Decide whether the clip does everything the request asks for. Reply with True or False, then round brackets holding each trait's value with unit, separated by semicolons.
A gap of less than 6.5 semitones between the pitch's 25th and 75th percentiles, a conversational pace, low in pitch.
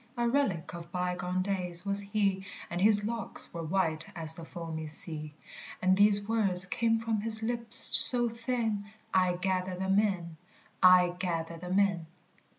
False (3.4 semitones; 155 wpm; 190 Hz)